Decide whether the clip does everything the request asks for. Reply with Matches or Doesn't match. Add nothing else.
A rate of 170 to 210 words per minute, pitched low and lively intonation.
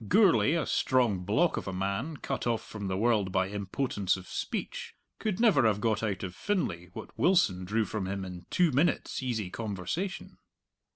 Matches